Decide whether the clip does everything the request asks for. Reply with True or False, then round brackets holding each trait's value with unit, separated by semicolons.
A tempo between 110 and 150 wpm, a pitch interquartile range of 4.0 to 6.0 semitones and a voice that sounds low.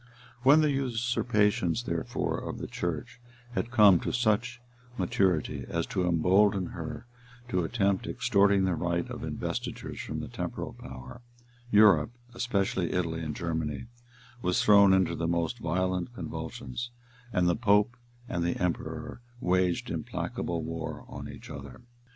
True (140 wpm; 4.8 semitones; 95 Hz)